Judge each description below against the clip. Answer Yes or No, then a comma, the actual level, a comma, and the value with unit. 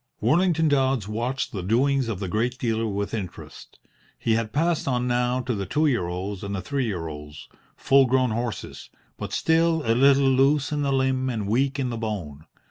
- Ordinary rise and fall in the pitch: Yes, average, 4.5 semitones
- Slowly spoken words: No, average, 195 wpm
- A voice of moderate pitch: No, low, 125 Hz